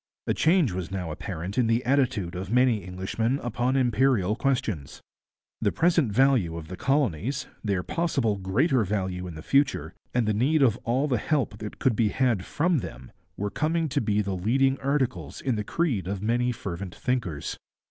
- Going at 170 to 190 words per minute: Yes, average, 180 wpm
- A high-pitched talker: No, low, 115 Hz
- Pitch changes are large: Yes, wide, 6.0 semitones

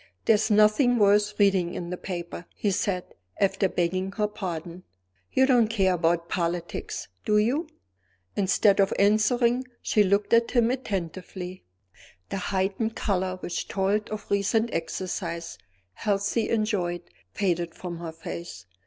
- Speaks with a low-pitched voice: No, high, 195 Hz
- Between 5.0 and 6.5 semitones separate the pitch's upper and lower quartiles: No, average, 3.3 semitones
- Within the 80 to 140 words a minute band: Yes, slow, 135 wpm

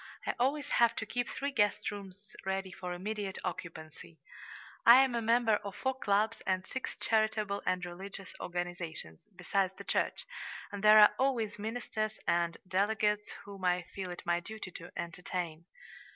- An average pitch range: Yes, average, 3.5 semitones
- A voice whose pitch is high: Yes, high, 200 Hz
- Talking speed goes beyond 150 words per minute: Yes, average, 160 wpm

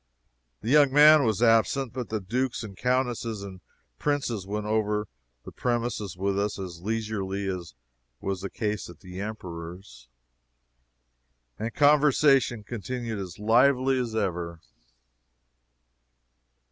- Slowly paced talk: Yes, slow, 120 wpm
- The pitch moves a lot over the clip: No, average, 4.3 semitones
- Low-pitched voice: Yes, low, 110 Hz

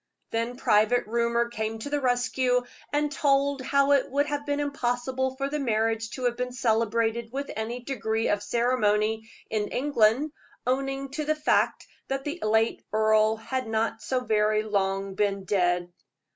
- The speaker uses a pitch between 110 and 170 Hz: No, high, 235 Hz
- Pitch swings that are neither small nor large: Yes, average, 3.8 semitones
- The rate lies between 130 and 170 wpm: Yes, average, 160 wpm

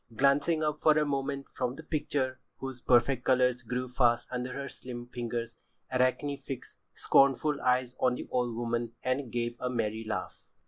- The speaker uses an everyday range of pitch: No, narrow, 2.3 semitones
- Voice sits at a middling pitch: No, low, 125 Hz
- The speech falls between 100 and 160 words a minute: No, average, 170 wpm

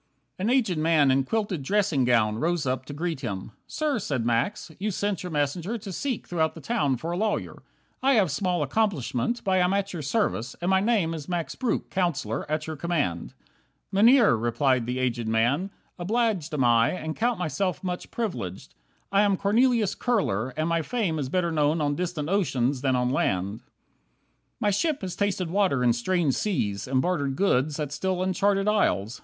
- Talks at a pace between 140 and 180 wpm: No, average, 190 wpm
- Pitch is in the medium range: Yes, medium, 170 Hz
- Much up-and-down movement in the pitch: Yes, wide, 7.0 semitones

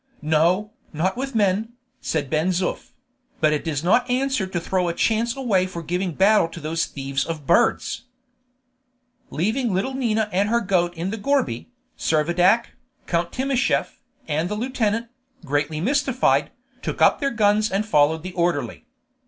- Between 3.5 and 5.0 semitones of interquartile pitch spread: No, wide, 5.5 semitones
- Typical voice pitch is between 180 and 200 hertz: Yes, high, 190 Hz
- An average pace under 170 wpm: Yes, average, 155 wpm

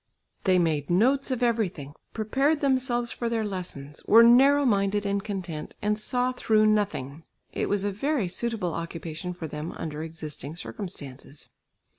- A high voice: Yes, high, 200 Hz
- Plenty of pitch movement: Yes, wide, 6.3 semitones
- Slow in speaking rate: No, average, 150 wpm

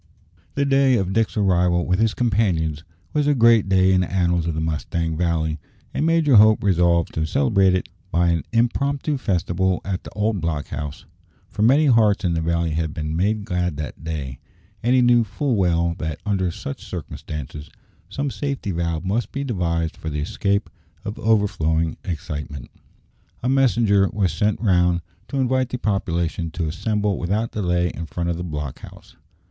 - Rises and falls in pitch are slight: No, average, 5.1 semitones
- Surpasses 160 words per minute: Yes, average, 175 wpm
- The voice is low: Yes, very low, 90 Hz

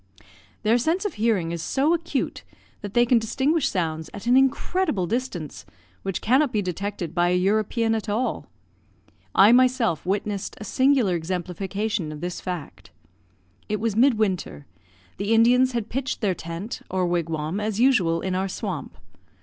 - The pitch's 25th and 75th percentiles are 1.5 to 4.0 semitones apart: No, average, 5.3 semitones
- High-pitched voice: Yes, high, 210 Hz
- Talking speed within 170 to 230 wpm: No, average, 160 wpm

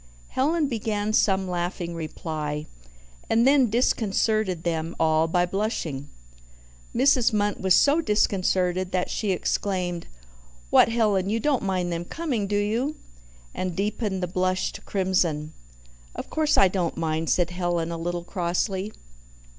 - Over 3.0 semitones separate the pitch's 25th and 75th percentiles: Yes, average, 3.9 semitones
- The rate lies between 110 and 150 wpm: Yes, average, 140 wpm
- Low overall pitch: No, medium, 185 Hz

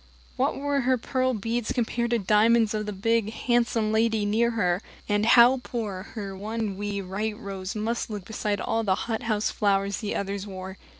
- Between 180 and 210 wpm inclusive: Yes, average, 185 wpm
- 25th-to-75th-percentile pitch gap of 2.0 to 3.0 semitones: Yes, narrow, 2.6 semitones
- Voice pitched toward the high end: Yes, high, 215 Hz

